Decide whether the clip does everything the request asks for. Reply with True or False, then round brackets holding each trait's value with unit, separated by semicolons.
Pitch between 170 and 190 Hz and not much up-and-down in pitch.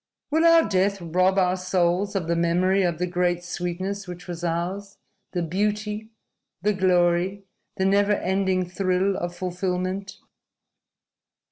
True (185 Hz; 1.9 semitones)